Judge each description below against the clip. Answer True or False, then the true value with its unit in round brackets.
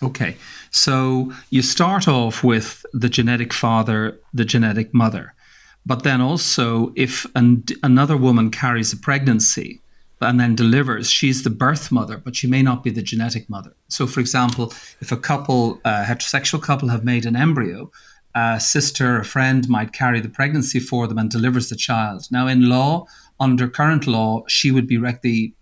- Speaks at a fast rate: False (180 wpm)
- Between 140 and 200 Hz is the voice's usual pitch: False (125 Hz)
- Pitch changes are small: True (2.2 semitones)